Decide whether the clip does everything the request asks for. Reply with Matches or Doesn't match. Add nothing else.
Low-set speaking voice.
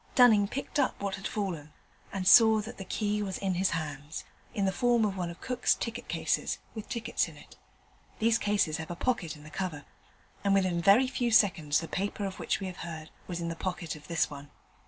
Doesn't match